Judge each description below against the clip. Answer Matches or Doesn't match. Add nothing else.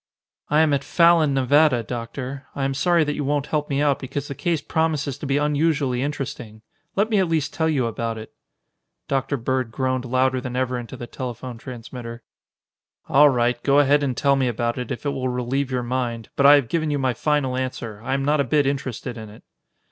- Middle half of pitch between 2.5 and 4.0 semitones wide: Matches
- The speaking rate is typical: Doesn't match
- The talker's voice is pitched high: Doesn't match